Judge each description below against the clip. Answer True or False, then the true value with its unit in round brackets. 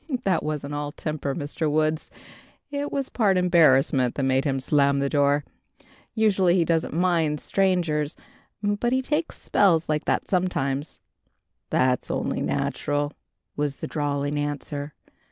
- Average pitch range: True (4.1 semitones)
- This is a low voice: False (150 Hz)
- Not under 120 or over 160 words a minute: True (135 wpm)